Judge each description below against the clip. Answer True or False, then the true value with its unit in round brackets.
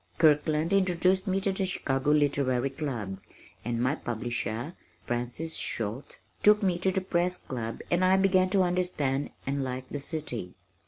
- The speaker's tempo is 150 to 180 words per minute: True (155 wpm)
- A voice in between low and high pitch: True (150 Hz)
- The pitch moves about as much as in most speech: False (6.3 semitones)